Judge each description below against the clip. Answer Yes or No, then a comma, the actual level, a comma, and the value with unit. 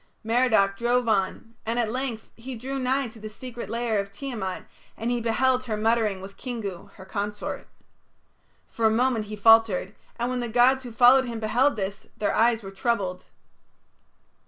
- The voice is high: Yes, high, 230 Hz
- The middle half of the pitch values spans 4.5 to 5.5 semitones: No, average, 2.8 semitones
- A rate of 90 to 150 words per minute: No, average, 175 wpm